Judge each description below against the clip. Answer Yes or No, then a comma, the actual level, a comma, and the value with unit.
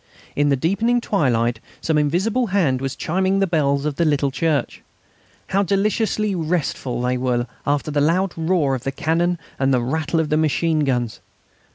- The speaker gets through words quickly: No, average, 175 wpm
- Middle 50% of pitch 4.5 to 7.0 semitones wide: Yes, average, 4.9 semitones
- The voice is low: No, medium, 155 Hz